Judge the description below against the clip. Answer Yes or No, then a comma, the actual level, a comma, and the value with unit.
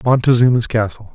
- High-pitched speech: No, low, 115 Hz